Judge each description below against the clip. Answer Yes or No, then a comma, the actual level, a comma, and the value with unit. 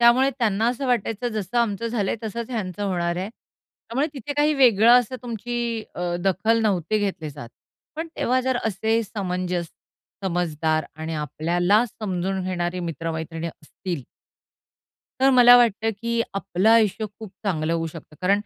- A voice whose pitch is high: Yes, high, 200 Hz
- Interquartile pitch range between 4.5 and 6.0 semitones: Yes, average, 5.0 semitones